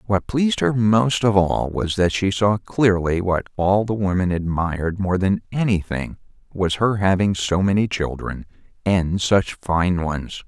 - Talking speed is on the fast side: No, average, 165 wpm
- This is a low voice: Yes, very low, 95 Hz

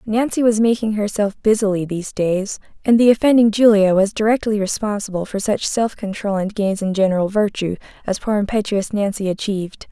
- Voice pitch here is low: No, high, 205 Hz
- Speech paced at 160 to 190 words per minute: Yes, average, 170 wpm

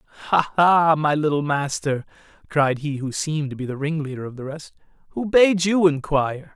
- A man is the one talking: Yes, male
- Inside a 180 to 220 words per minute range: Yes, average, 185 wpm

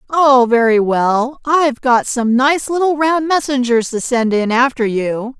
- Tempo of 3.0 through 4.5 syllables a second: Yes, 4.1 syllables/s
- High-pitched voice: Yes, very high, 255 Hz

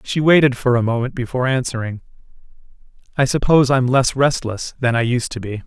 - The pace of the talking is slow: No, average, 180 wpm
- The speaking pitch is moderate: No, low, 125 Hz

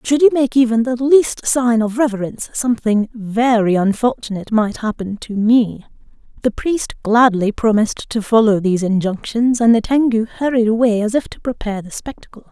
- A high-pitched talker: Yes, high, 230 Hz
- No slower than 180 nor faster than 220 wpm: No, average, 170 wpm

